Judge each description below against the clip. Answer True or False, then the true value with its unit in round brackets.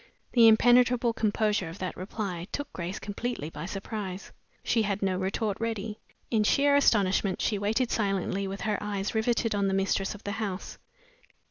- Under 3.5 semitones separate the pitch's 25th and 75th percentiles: True (2.6 semitones)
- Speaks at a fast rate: False (165 wpm)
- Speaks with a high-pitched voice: True (205 Hz)